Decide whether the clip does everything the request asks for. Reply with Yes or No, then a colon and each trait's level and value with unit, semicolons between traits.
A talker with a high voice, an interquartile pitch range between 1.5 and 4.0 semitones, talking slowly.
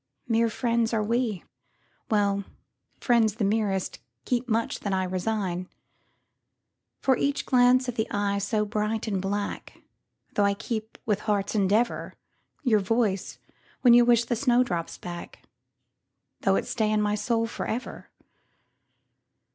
Yes: high, 215 Hz; average, 2.8 semitones; slow, 120 wpm